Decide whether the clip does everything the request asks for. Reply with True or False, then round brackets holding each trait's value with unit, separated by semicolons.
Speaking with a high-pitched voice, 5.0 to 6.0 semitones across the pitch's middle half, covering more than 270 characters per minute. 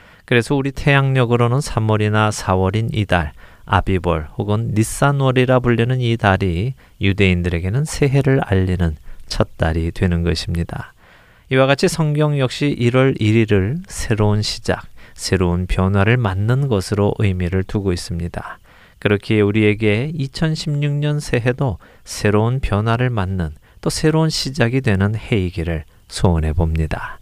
False (105 Hz; 5.5 semitones; 290 characters per minute)